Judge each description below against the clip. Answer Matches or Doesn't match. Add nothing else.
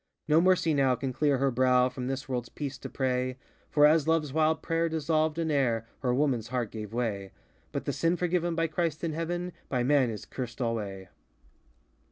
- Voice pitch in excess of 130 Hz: Matches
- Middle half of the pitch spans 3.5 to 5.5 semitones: Matches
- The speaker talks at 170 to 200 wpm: Matches